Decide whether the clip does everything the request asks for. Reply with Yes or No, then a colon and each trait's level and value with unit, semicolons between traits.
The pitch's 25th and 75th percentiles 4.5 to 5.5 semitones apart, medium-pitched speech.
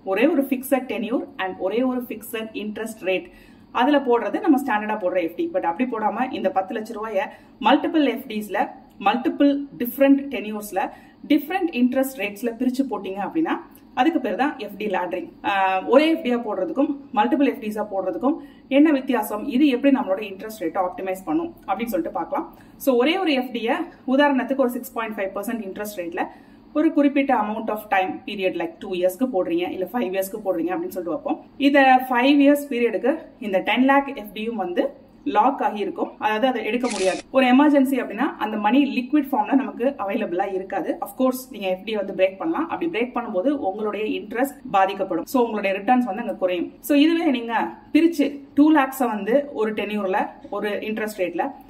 No: average, 5.0 semitones; very high, 255 Hz